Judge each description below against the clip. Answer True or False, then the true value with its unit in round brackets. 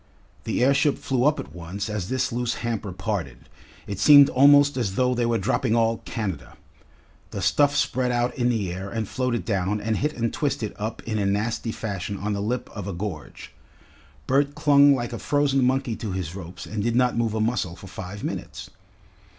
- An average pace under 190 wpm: False (200 wpm)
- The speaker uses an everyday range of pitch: True (4.3 semitones)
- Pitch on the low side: True (115 Hz)